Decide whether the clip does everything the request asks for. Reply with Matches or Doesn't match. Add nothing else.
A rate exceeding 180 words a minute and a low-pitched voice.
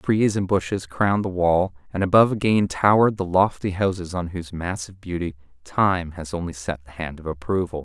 Matches